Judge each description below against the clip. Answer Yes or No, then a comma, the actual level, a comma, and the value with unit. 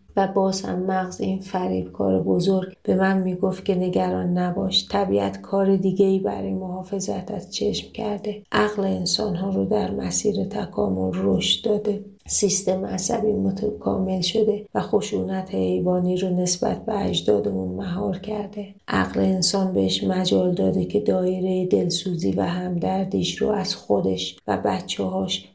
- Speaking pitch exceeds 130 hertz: Yes, medium, 185 Hz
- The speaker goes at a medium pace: Yes, average, 145 wpm